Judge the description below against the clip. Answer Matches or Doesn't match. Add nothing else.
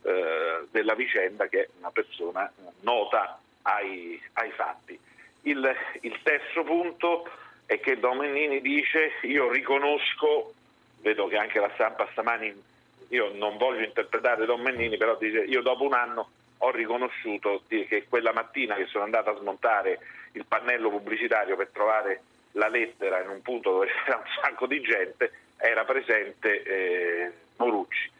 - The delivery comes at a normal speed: Matches